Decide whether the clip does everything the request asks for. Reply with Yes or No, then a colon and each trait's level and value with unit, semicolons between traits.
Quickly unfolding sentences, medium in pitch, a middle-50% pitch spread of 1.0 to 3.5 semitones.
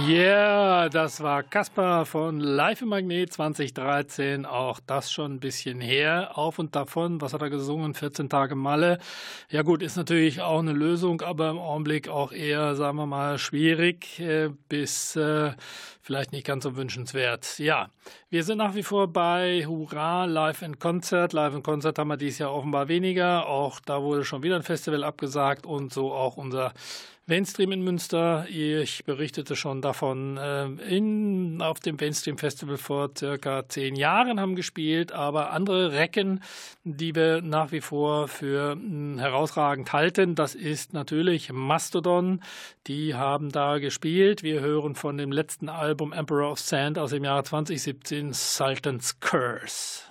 No: average, 160 wpm; medium, 150 Hz; average, 3.0 semitones